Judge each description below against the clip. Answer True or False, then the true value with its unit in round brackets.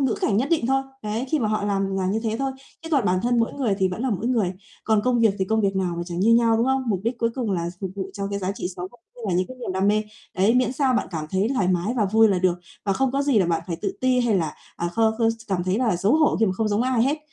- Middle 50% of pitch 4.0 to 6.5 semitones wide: True (4.4 semitones)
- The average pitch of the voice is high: True (215 Hz)